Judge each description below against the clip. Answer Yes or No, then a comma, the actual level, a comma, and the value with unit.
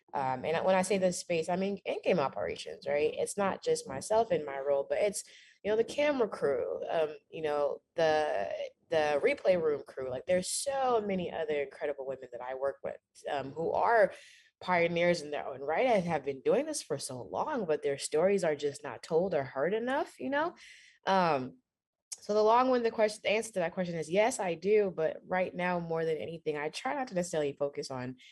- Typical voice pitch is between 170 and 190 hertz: Yes, medium, 185 Hz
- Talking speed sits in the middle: No, fast, 215 wpm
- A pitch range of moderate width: No, wide, 8.2 semitones